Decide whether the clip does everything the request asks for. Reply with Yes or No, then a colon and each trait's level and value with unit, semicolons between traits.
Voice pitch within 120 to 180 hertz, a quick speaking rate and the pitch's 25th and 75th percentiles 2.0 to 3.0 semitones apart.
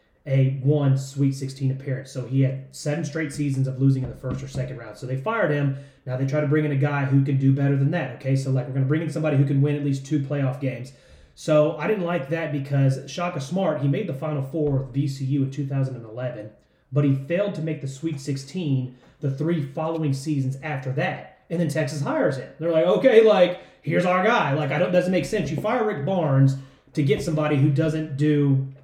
Yes: medium, 140 Hz; fast, 235 wpm; average, 2.7 semitones